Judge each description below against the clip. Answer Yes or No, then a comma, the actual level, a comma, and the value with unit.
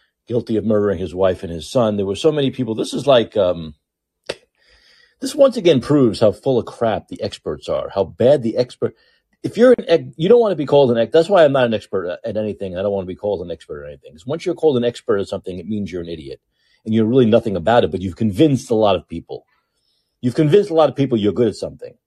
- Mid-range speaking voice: No, low, 115 Hz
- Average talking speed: No, fast, 265 wpm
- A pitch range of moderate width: No, wide, 8.1 semitones